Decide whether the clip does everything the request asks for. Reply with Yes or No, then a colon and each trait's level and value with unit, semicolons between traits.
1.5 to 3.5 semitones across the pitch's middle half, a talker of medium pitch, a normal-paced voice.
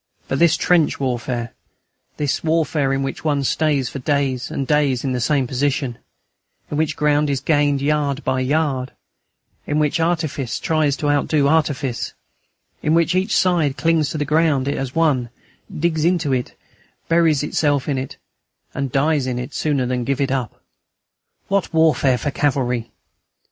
Yes: average, 2.9 semitones; medium, 145 Hz; average, 165 wpm